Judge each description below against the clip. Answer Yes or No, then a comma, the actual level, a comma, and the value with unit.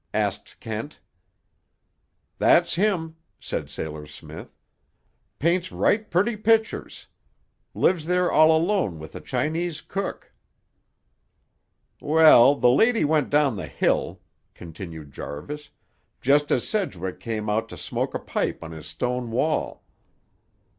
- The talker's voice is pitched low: No, medium, 150 Hz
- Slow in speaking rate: Yes, slow, 120 wpm